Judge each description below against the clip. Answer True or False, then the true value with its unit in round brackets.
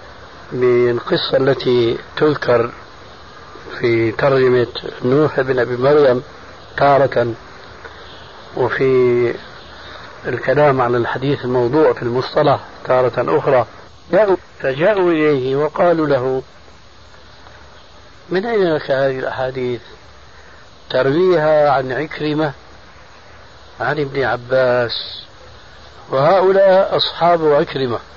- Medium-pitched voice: False (130 Hz)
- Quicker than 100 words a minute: False (80 wpm)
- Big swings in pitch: False (3.5 semitones)